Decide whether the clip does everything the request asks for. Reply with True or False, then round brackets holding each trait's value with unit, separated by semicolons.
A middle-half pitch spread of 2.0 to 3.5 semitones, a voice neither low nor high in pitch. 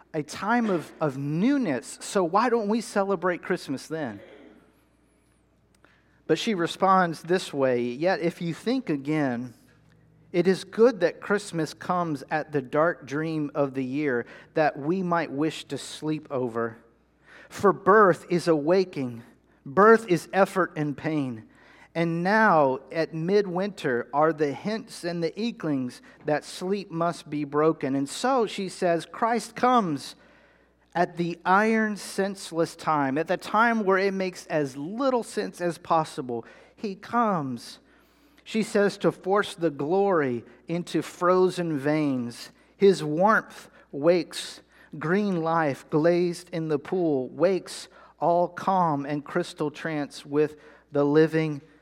False (4.3 semitones; 165 Hz)